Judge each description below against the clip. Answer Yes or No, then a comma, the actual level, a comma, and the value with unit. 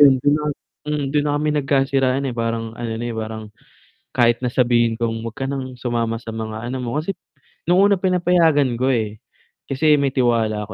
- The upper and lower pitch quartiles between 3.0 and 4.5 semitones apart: Yes, average, 4.0 semitones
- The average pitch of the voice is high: No, low, 125 Hz